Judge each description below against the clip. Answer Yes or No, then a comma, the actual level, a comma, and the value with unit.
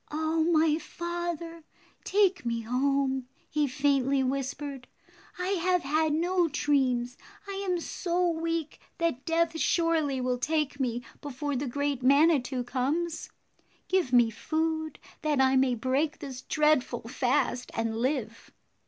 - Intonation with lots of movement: No, average, 4.2 semitones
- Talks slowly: Yes, slow, 130 wpm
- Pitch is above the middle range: Yes, very high, 290 Hz